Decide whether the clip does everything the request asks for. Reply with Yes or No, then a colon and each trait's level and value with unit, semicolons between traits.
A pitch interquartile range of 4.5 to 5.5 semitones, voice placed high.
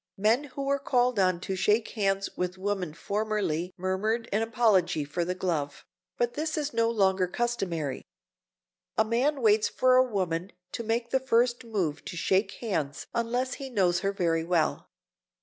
Yes: average, 4.8 semitones; high, 205 Hz